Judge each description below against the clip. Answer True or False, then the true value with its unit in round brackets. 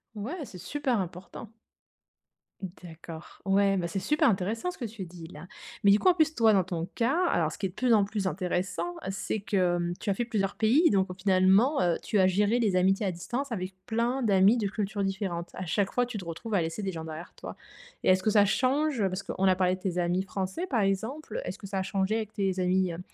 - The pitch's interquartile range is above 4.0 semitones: False (3.6 semitones)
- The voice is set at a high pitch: True (195 Hz)